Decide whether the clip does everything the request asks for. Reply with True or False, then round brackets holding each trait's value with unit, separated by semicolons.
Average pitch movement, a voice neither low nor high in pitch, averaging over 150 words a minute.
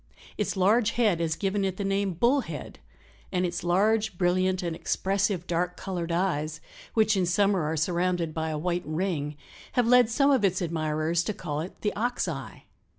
True (3.3 semitones; 180 Hz; 185 wpm)